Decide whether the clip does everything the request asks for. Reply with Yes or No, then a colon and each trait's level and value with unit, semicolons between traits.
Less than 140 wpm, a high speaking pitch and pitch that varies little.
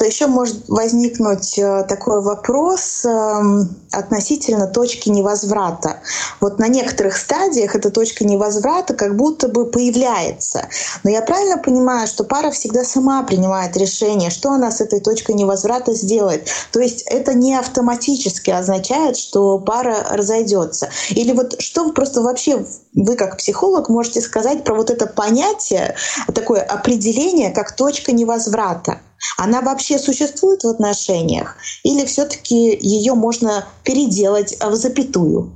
No: average, 130 wpm; high, 230 Hz; average, 4.2 semitones